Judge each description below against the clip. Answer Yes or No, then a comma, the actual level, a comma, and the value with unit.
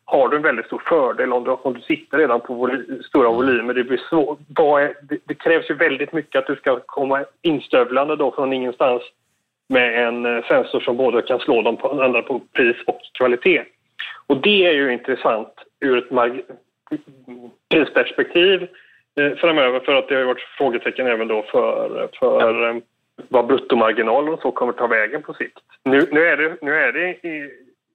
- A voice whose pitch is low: No, medium, 145 Hz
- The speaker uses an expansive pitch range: Yes, wide, 6.0 semitones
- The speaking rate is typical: Yes, average, 180 wpm